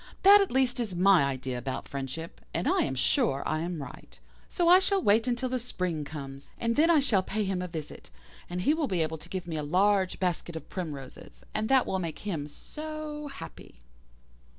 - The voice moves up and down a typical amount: No, wide, 8.4 semitones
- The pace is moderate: No, fast, 210 wpm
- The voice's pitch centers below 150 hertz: No, medium, 185 Hz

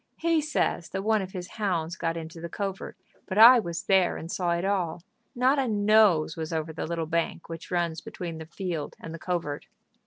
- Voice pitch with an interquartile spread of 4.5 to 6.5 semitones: No, average, 3.7 semitones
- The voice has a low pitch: No, medium, 175 Hz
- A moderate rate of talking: No, fast, 210 wpm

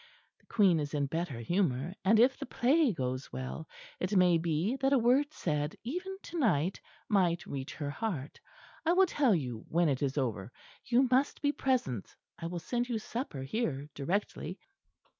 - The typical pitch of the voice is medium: Yes, medium, 180 Hz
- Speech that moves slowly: No, average, 180 wpm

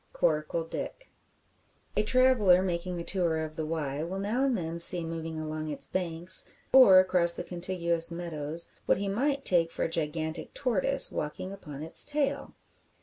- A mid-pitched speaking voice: Yes, medium, 170 Hz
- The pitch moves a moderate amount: Yes, average, 3.5 semitones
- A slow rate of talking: No, average, 165 wpm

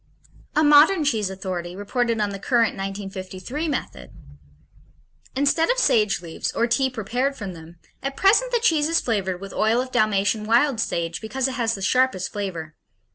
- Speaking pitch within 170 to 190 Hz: No, high, 220 Hz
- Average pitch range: No, wide, 5.8 semitones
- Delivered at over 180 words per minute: No, average, 170 wpm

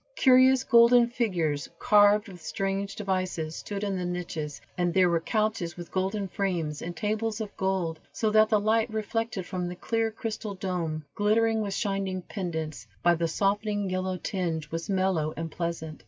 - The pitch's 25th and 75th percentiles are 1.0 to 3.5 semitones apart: No, average, 3.9 semitones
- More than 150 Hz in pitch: Yes, high, 190 Hz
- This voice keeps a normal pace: Yes, average, 170 wpm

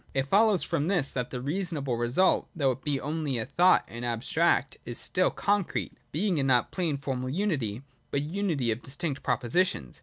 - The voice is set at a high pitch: No, medium, 140 Hz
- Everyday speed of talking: Yes, average, 195 wpm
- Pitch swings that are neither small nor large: No, wide, 5.8 semitones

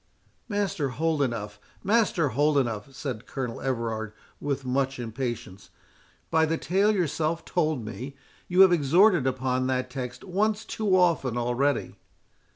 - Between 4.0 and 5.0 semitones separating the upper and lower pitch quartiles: No, wide, 5.6 semitones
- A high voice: No, medium, 140 Hz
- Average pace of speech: No, slow, 125 wpm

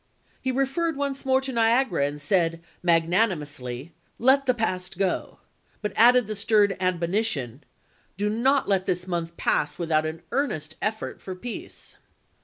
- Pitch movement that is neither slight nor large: No, wide, 6.7 semitones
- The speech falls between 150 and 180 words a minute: Yes, average, 155 wpm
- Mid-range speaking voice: No, high, 195 Hz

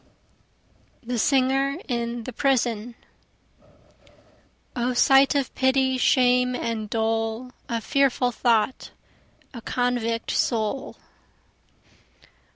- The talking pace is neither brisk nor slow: No, slow, 85 wpm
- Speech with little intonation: Yes, narrow, 2.3 semitones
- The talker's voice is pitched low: No, high, 245 Hz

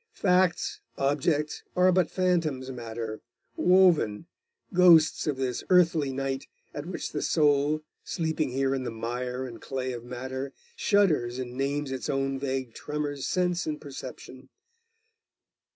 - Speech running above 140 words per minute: No, slow, 135 wpm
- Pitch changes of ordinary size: Yes, average, 4.0 semitones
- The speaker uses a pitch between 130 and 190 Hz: Yes, medium, 140 Hz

